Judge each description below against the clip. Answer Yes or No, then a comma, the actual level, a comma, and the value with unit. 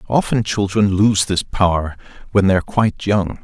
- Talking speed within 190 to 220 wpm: No, average, 175 wpm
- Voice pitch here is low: Yes, low, 100 Hz